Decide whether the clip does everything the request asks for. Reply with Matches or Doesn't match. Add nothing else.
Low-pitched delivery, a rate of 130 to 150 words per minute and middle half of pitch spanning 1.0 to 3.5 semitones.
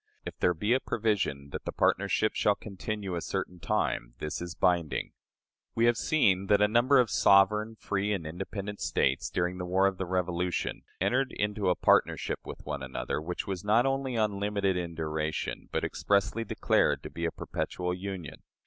Doesn't match